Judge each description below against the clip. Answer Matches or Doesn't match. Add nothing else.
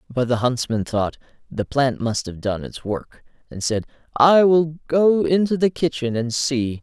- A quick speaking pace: Doesn't match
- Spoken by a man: Matches